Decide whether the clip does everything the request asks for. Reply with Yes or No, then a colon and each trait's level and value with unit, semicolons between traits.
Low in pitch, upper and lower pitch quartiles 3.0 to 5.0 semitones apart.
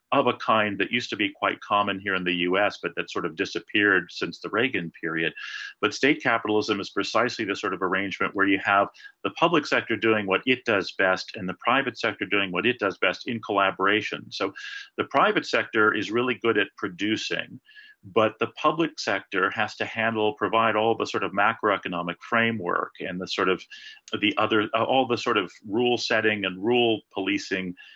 Yes: low, 110 Hz; average, 3.4 semitones